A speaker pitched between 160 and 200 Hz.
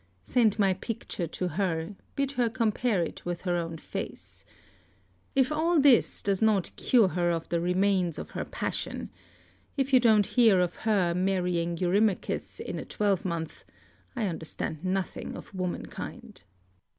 Yes: high, 190 Hz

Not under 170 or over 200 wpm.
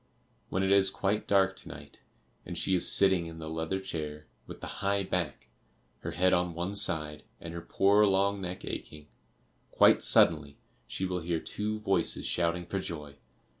Yes: average, 175 wpm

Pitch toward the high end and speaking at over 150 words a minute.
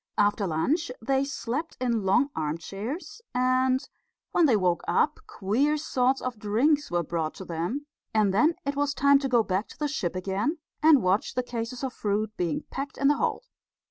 Yes: high, 245 Hz; average, 185 wpm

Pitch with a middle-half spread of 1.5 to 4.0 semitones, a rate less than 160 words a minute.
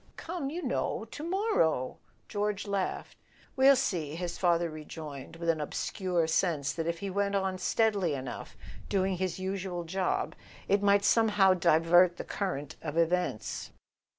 Yes: average, 3.4 semitones; average, 150 wpm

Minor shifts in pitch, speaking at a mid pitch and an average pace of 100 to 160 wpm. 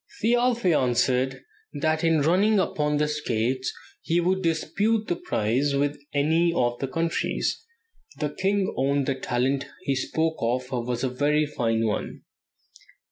No: average, 4.5 semitones; medium, 145 Hz; average, 140 wpm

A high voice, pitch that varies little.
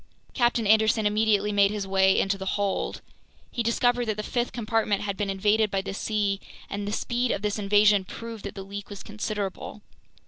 Yes: high, 210 Hz; narrow, 1.7 semitones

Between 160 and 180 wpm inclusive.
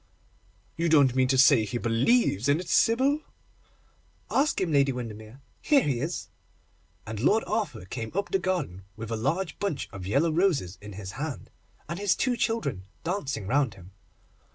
Yes: average, 175 wpm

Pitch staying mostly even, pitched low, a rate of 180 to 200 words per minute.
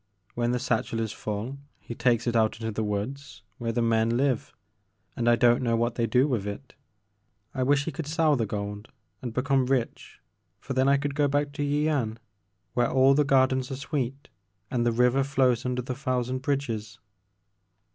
No: average, 3.0 semitones; low, 125 Hz; average, 190 wpm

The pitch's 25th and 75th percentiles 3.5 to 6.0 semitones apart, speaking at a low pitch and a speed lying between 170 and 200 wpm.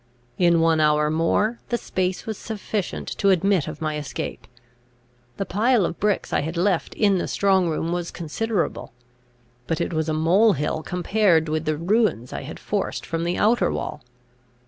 No: average, 4.3 semitones; medium, 175 Hz; average, 175 wpm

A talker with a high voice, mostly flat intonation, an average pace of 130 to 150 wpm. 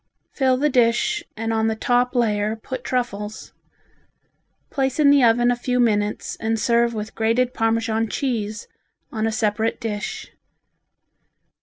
Yes: high, 230 Hz; narrow, 2.2 semitones; average, 140 wpm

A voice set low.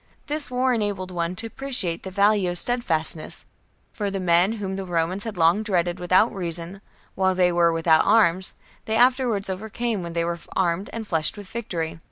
No: high, 190 Hz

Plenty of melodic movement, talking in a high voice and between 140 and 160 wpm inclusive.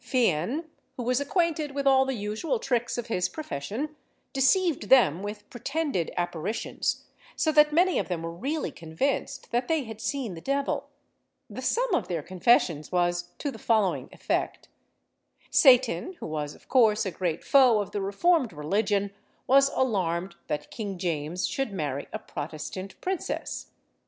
Yes: wide, 7.7 semitones; high, 225 Hz; average, 155 wpm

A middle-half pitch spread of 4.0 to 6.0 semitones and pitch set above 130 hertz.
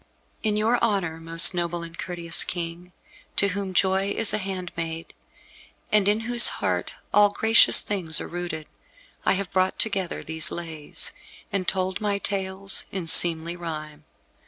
No: average, 3.1 semitones; medium, 185 Hz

